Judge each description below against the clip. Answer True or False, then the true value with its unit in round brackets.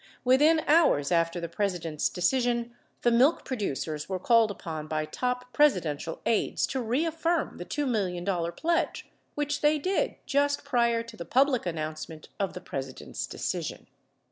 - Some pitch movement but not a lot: False (9.0 semitones)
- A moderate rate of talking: True (145 wpm)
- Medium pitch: False (230 Hz)